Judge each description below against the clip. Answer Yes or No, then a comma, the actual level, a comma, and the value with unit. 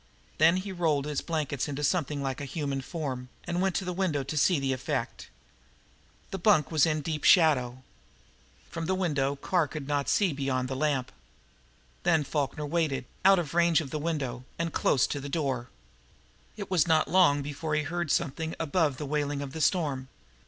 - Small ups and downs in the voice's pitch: No, average, 3.3 semitones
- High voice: No, medium, 150 Hz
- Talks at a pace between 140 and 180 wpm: No, average, 190 wpm